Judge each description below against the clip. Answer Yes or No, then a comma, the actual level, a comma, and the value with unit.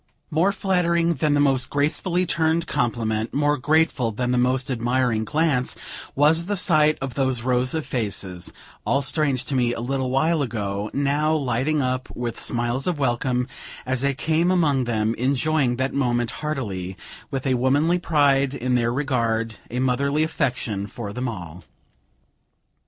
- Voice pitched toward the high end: No, low, 130 Hz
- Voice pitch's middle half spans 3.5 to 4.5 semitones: Yes, average, 3.9 semitones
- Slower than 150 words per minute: No, average, 155 wpm